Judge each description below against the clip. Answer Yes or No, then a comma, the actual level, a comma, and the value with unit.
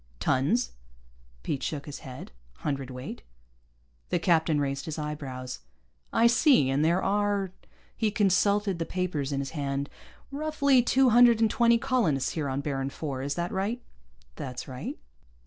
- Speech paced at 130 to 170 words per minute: Yes, average, 150 wpm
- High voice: No, medium, 160 Hz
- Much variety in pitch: Yes, wide, 7.7 semitones